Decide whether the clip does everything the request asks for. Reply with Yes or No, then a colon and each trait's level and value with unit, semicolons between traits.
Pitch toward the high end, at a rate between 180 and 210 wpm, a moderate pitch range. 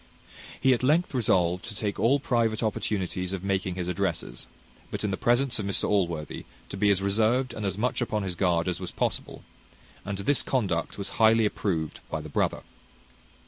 No: low, 100 Hz; average, 185 wpm; average, 4.0 semitones